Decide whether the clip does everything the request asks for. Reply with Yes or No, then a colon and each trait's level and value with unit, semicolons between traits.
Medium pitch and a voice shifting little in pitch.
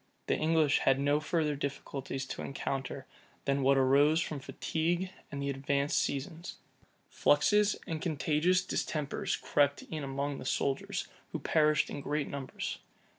Yes: medium, 145 Hz; narrow, 2.3 semitones